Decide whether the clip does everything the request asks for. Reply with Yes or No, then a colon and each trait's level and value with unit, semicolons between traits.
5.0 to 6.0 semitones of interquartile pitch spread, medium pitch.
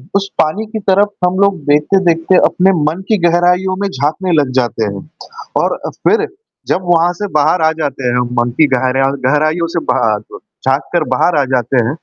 Yes: wide, 5.4 semitones; medium, 165 Hz